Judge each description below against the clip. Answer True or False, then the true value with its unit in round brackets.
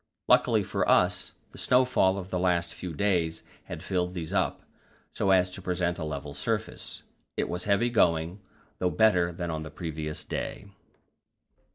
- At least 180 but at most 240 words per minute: False (165 wpm)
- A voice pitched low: True (90 Hz)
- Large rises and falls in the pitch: False (3.0 semitones)